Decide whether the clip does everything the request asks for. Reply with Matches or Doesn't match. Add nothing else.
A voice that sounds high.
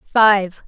Matches